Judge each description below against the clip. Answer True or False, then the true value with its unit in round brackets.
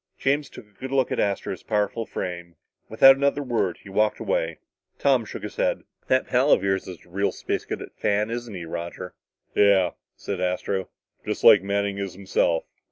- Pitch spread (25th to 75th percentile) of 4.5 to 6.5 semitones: True (4.9 semitones)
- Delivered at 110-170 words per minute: False (185 wpm)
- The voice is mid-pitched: False (100 Hz)